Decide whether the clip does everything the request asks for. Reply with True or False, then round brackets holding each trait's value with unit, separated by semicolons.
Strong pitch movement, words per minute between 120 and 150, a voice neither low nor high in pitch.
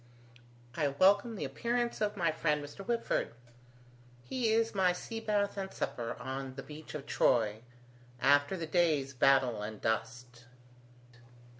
True (7.4 semitones; 140 wpm; 150 Hz)